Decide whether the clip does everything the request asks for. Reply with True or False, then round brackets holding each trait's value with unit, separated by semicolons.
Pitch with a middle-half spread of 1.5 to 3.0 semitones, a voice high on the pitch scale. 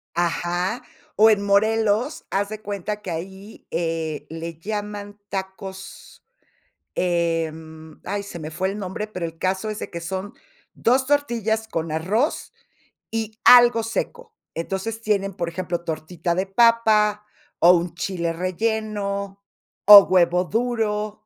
False (3.9 semitones; 195 Hz)